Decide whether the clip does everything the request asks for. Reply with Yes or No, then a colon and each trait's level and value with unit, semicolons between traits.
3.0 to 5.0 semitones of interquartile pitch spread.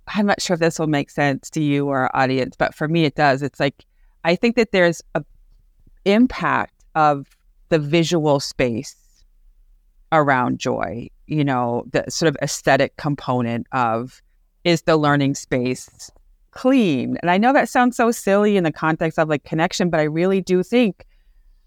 No: wide, 5.6 semitones